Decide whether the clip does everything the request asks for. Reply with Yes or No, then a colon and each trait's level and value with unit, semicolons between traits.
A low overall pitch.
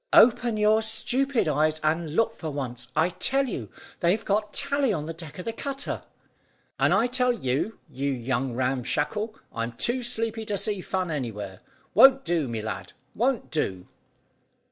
No: medium, 180 Hz